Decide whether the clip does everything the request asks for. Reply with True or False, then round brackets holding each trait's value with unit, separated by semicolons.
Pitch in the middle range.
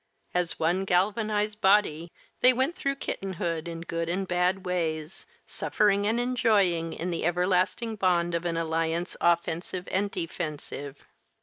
True (180 Hz)